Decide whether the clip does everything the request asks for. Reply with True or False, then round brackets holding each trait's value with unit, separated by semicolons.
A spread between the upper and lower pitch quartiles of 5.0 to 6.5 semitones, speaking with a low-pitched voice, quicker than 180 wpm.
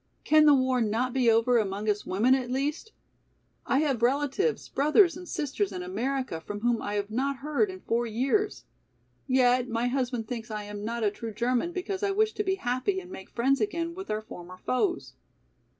False (5.4 semitones; 255 Hz; 200 wpm)